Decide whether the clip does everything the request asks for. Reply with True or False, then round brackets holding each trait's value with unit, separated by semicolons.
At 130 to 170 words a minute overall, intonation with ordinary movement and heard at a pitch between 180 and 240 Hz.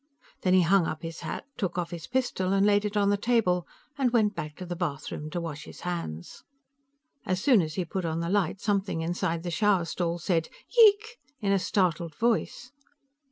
False (205 wpm; 3.6 semitones; 185 Hz)